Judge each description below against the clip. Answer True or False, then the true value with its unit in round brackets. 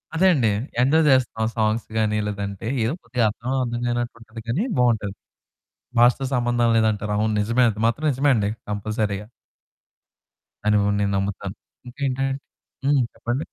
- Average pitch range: True (3.0 semitones)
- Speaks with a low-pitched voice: True (115 Hz)